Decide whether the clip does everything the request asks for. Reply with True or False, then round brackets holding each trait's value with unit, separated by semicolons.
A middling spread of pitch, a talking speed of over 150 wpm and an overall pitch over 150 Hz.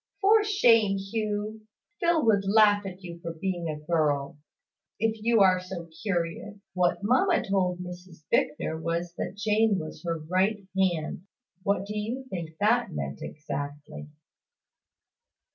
False (4.1 semitones; 140 wpm; 190 Hz)